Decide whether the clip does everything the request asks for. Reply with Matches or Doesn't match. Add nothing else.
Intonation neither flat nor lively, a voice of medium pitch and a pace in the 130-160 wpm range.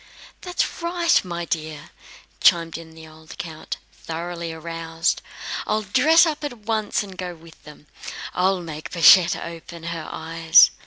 Matches